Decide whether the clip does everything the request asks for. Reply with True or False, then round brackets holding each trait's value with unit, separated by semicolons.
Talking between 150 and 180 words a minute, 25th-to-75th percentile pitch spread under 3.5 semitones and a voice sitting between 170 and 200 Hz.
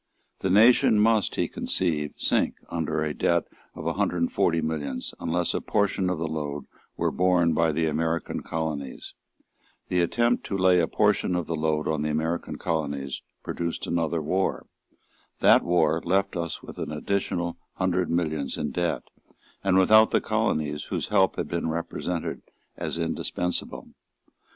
False (160 wpm; 2.8 semitones; 85 Hz)